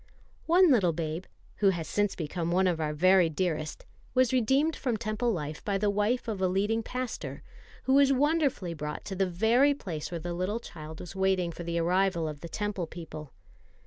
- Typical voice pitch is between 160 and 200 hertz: Yes, high, 190 Hz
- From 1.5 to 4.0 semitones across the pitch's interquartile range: No, average, 5.1 semitones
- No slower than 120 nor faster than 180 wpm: No, average, 195 wpm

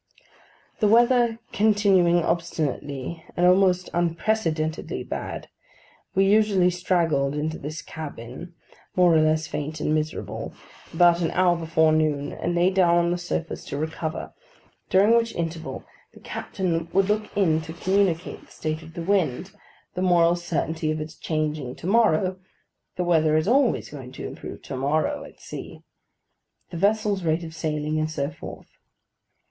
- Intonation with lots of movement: No, average, 3.1 semitones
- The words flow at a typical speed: Yes, average, 155 wpm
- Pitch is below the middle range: No, medium, 170 Hz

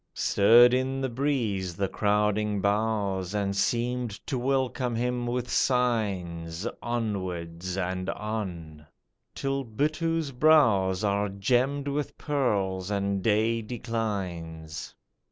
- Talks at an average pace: No, slow, 105 wpm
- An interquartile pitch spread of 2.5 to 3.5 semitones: No, average, 4.5 semitones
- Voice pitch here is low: Yes, low, 105 Hz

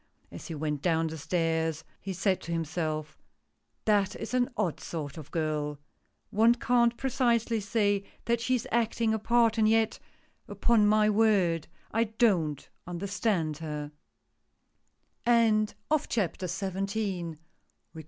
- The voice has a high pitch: Yes, high, 200 Hz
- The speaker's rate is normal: No, slow, 125 wpm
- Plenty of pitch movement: Yes, wide, 5.8 semitones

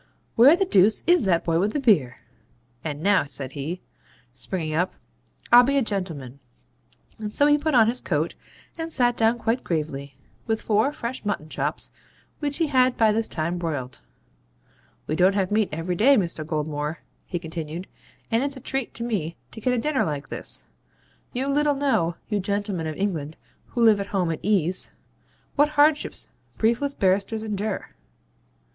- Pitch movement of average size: No, wide, 7.0 semitones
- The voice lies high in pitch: Yes, high, 205 Hz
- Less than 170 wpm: No, average, 175 wpm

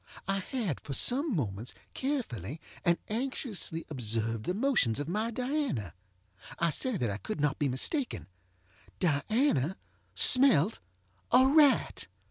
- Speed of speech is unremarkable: No, slow, 115 wpm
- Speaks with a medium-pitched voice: Yes, medium, 165 Hz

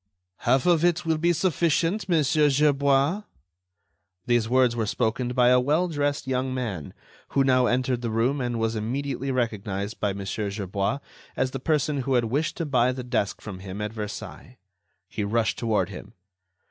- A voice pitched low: Yes, low, 125 Hz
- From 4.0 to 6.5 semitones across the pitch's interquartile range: Yes, average, 4.4 semitones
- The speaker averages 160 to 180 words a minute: Yes, average, 170 wpm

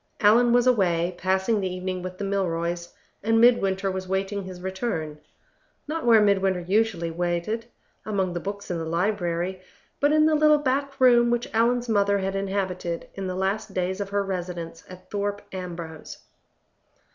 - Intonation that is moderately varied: Yes, average, 3.5 semitones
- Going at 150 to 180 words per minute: Yes, average, 165 wpm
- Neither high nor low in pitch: No, high, 195 Hz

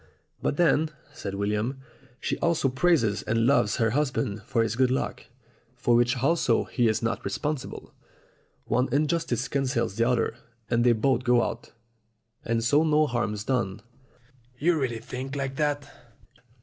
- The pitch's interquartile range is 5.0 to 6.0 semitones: No, average, 3.6 semitones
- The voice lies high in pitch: No, low, 125 Hz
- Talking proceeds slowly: No, average, 150 wpm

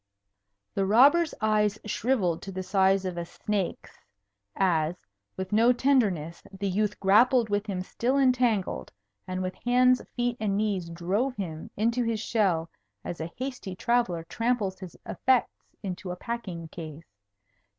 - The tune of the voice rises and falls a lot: No, average, 4.6 semitones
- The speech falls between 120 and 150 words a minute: Yes, average, 145 wpm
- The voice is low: No, high, 200 Hz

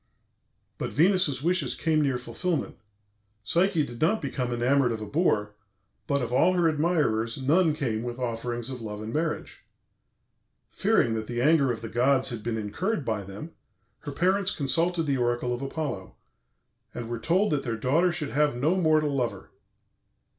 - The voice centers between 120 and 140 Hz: Yes, low, 135 Hz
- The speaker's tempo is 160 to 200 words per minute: Yes, average, 170 wpm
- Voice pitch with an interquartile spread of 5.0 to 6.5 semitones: Yes, wide, 5.4 semitones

